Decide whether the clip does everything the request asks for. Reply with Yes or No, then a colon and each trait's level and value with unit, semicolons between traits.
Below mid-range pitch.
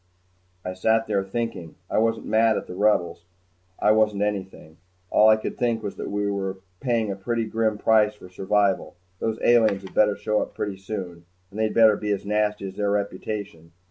Yes: low, 105 Hz